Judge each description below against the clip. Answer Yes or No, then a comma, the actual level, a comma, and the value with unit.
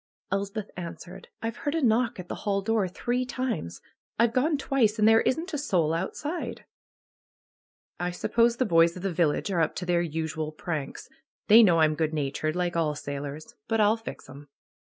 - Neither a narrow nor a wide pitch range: No, wide, 6.4 semitones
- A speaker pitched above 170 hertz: Yes, medium, 185 Hz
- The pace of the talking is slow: No, average, 180 wpm